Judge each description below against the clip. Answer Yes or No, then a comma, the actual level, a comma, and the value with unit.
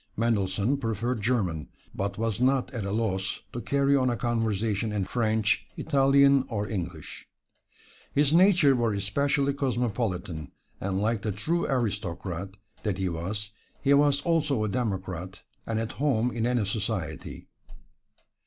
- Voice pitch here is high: No, low, 115 Hz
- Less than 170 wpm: Yes, average, 140 wpm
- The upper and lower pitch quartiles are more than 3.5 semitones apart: Yes, average, 5.0 semitones